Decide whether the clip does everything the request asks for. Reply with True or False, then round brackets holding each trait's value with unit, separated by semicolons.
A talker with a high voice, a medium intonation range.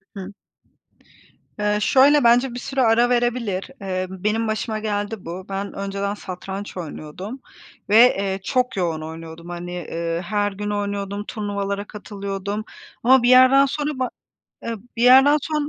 True (205 Hz; 4.0 semitones)